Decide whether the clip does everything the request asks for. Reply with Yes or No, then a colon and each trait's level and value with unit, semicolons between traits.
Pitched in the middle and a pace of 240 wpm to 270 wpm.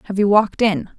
No: high, 200 Hz; fast, 245 wpm